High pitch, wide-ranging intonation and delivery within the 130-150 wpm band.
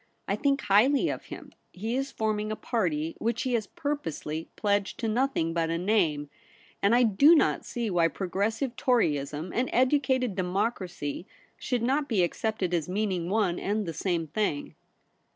No: high, 210 Hz; wide, 5.9 semitones; average, 165 wpm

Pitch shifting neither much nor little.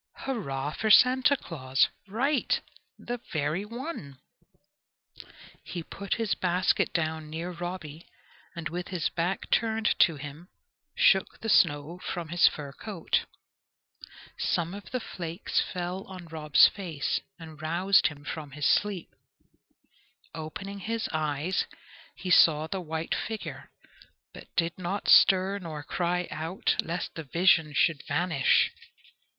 Yes: average, 3.7 semitones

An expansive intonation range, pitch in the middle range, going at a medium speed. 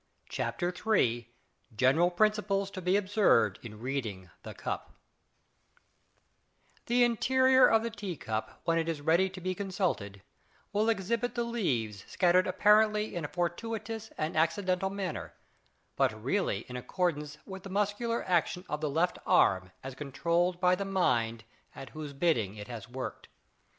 Yes: wide, 7.4 semitones; medium, 175 Hz; average, 150 wpm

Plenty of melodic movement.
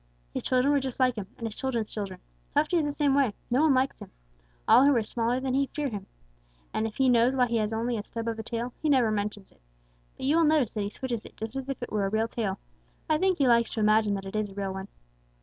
No: average, 3.9 semitones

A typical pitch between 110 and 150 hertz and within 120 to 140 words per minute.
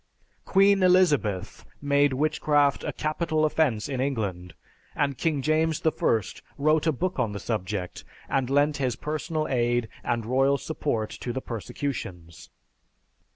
Yes: medium, 140 Hz; slow, 135 wpm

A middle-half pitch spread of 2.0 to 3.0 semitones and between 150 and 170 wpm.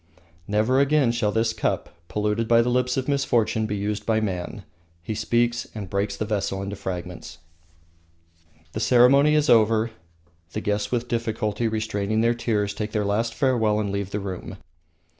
Yes: narrow, 2.5 semitones; average, 165 wpm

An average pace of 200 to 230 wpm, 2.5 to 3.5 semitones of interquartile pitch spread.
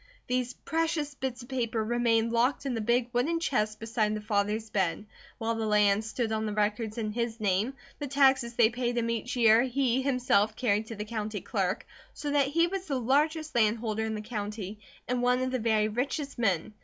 Yes: fast, 205 wpm; average, 3.1 semitones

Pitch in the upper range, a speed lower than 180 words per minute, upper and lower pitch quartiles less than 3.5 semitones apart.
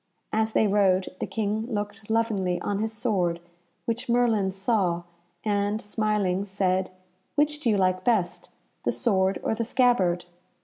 Yes: high, 205 Hz; average, 145 wpm; average, 3.0 semitones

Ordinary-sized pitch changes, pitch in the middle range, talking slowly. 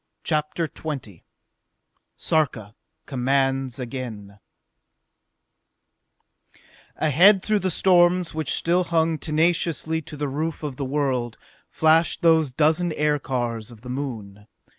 Yes: average, 4.2 semitones; medium, 150 Hz; slow, 105 wpm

